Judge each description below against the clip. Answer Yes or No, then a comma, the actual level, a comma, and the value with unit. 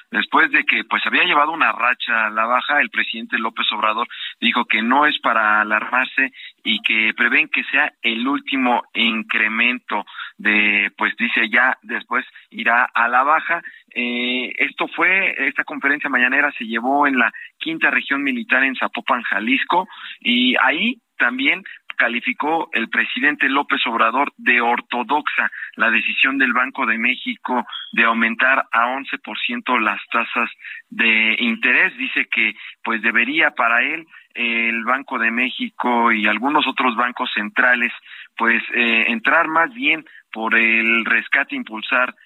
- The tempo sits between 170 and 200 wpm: No, average, 145 wpm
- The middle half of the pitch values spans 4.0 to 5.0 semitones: Yes, average, 4.6 semitones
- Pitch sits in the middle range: No, low, 125 Hz